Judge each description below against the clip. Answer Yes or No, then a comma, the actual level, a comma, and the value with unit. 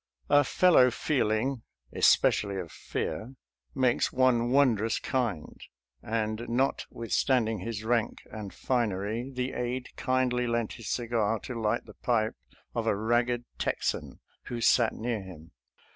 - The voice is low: Yes, low, 120 Hz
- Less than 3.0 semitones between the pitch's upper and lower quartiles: Yes, narrow, 2.6 semitones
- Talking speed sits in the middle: Yes, average, 145 wpm